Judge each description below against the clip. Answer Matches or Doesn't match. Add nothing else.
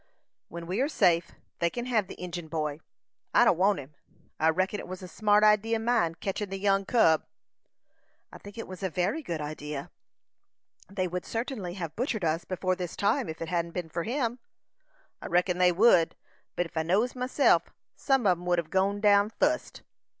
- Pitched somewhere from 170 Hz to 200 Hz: Matches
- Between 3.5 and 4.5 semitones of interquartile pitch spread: Matches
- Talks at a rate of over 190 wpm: Matches